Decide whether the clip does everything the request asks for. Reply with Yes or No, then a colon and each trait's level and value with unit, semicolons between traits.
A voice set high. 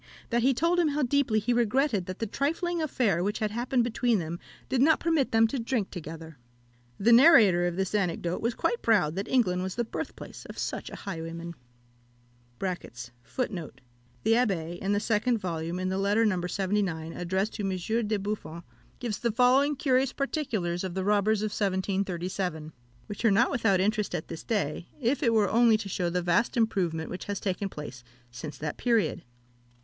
Yes: high, 205 Hz